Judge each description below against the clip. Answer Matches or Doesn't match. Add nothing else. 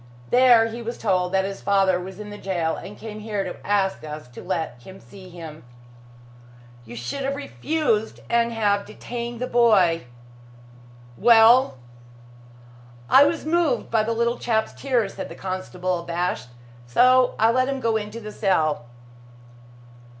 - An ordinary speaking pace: Matches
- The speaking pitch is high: Matches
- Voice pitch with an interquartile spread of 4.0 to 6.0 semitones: Matches